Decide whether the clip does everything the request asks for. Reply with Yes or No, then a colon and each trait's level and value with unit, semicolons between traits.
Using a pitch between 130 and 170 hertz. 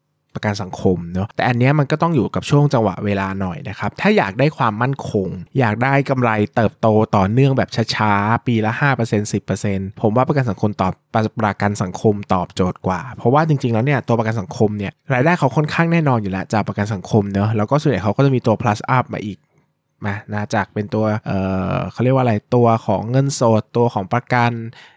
No: low, 110 Hz